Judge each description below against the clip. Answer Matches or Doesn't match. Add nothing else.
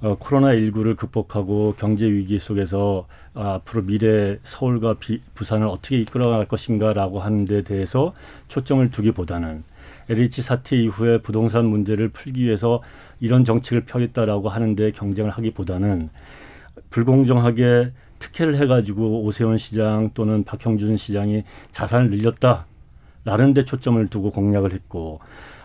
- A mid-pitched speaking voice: Doesn't match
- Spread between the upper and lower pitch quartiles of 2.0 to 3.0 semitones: Matches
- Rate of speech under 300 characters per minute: Doesn't match